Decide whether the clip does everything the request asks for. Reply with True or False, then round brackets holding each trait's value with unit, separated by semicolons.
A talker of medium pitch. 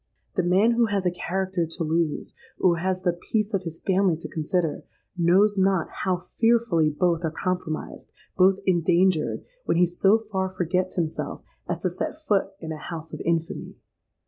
True (180 Hz)